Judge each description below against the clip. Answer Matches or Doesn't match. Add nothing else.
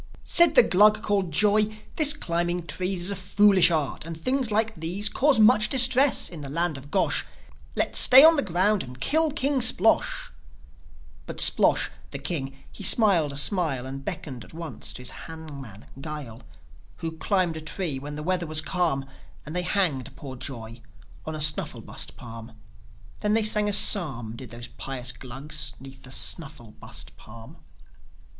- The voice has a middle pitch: Matches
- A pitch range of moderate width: Doesn't match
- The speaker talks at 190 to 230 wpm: Doesn't match